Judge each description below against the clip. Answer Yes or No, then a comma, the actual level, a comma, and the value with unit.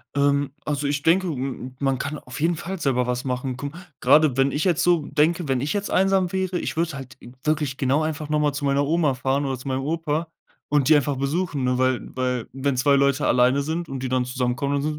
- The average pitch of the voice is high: No, medium, 140 Hz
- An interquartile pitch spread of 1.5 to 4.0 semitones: Yes, average, 3.0 semitones